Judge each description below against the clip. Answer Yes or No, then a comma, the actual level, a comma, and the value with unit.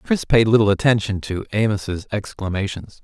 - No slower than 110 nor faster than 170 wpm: Yes, average, 140 wpm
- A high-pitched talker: No, low, 105 Hz